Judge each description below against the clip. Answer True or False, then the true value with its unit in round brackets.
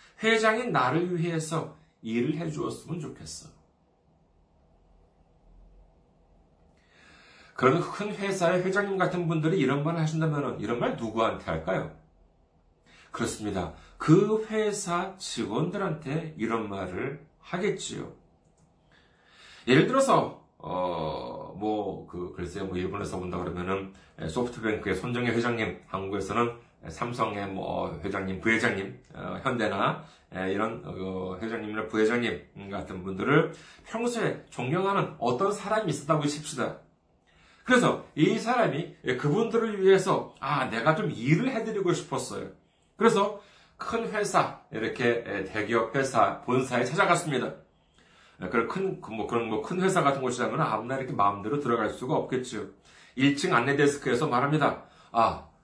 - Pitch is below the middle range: True (120 Hz)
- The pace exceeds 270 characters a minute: True (280 characters per minute)